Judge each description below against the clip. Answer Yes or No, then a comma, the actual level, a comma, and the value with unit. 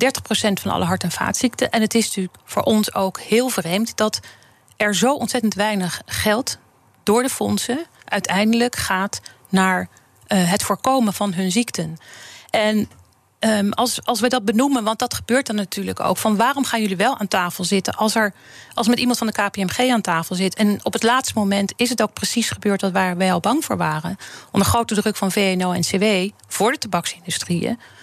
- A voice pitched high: Yes, high, 210 Hz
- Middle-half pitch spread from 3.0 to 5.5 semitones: Yes, average, 3.7 semitones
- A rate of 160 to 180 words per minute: No, average, 195 wpm